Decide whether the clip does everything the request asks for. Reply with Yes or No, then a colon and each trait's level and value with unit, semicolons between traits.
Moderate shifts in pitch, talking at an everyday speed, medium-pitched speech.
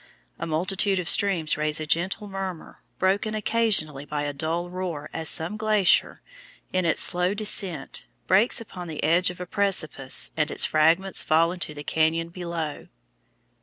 Yes: average, 3.6 semitones; average, 160 wpm; medium, 175 Hz